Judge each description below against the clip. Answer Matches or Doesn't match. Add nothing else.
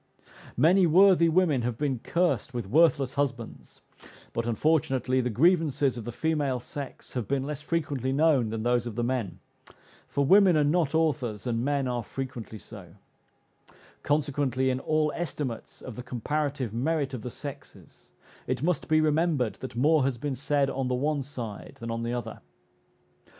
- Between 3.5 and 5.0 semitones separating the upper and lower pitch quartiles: Matches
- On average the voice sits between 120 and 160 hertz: Matches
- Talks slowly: Doesn't match